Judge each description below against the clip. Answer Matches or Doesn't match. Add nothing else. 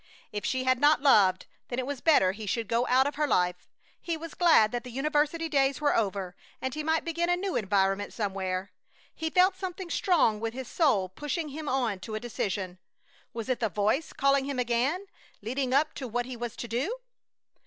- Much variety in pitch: Matches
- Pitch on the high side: Matches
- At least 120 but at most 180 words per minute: Doesn't match